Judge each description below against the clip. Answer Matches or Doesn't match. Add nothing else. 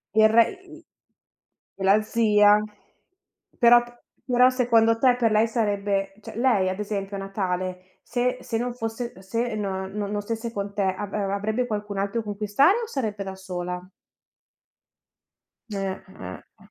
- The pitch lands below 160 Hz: Doesn't match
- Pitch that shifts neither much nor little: Matches